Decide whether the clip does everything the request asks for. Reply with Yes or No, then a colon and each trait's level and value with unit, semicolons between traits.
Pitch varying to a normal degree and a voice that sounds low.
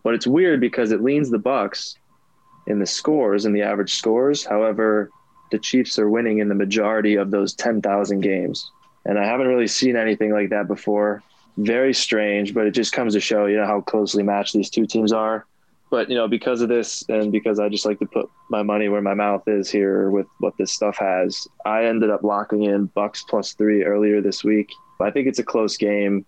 No: narrow, 1.4 semitones; low, 105 Hz